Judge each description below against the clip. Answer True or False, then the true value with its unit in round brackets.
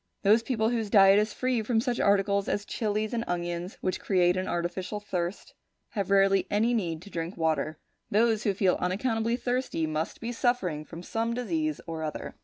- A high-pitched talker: True (200 Hz)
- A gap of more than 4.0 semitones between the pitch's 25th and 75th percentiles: True (4.5 semitones)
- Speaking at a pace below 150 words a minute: False (185 wpm)